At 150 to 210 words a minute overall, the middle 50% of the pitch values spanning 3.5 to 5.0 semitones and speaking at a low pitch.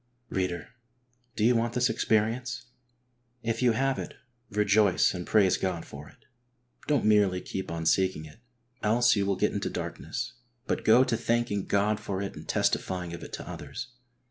Yes: average, 170 wpm; average, 4.0 semitones; low, 105 Hz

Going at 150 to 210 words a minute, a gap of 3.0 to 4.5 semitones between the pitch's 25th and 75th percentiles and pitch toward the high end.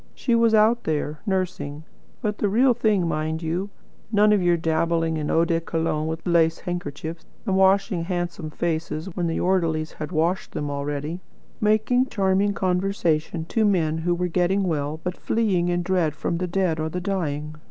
No: average, 175 wpm; average, 3.3 semitones; medium, 175 Hz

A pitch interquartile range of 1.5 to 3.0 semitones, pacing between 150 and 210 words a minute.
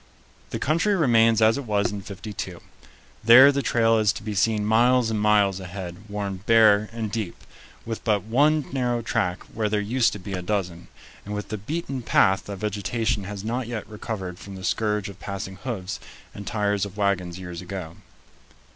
Yes: average, 2.7 semitones; average, 185 wpm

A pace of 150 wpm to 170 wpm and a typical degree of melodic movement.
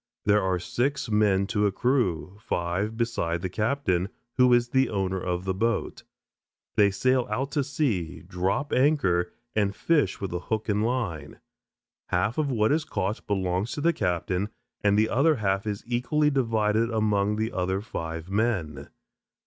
Yes: average, 160 wpm; average, 4.5 semitones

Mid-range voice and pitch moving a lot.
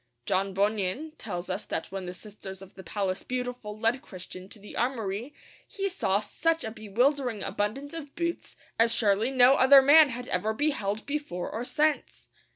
No: high, 220 Hz; wide, 5.9 semitones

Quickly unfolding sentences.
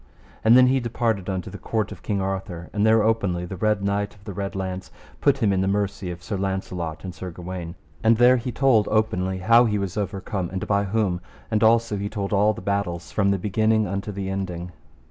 Yes: fast, 220 wpm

